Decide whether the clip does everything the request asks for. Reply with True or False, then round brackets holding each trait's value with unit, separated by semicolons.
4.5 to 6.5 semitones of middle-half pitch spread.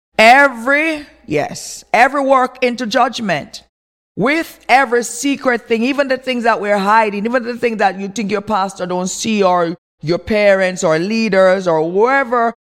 True (4.8 semitones)